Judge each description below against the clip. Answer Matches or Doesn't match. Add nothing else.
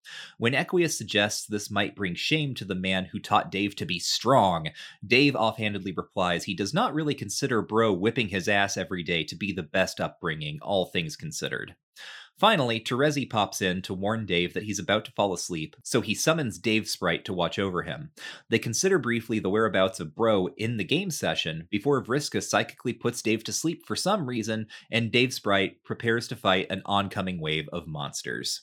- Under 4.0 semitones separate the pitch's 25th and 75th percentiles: Doesn't match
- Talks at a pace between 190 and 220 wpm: Matches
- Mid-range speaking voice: Doesn't match